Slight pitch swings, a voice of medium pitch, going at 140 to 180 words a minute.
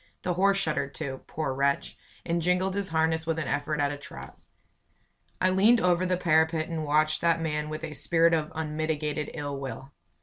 No: narrow, 2.1 semitones; medium, 160 Hz; average, 190 wpm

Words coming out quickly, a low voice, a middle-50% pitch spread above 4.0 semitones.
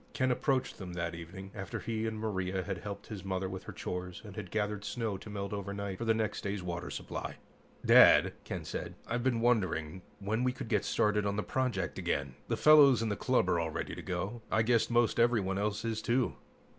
No: fast, 220 wpm; low, 105 Hz; average, 3.5 semitones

